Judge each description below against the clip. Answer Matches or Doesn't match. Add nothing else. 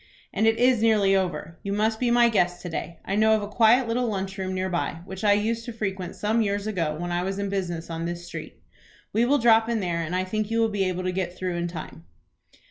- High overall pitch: Matches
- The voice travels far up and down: Doesn't match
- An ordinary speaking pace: Doesn't match